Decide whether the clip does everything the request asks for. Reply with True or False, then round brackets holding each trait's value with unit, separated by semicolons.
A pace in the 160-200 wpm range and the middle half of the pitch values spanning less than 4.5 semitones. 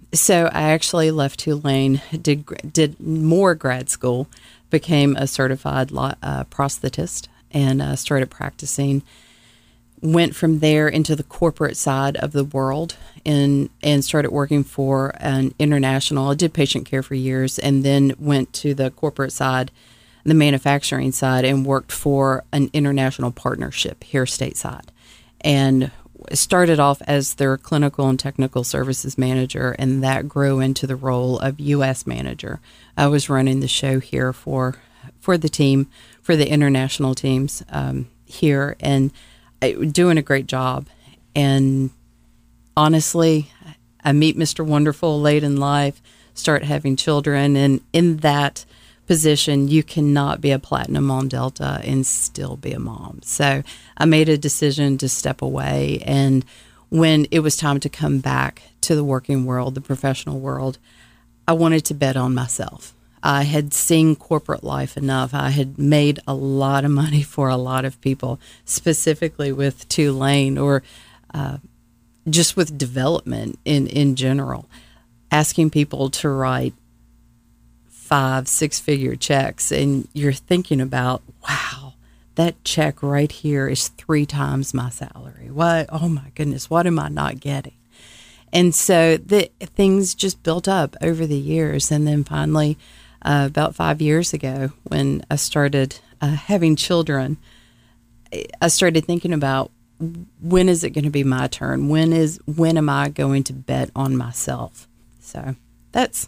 False (150 wpm; 2.5 semitones)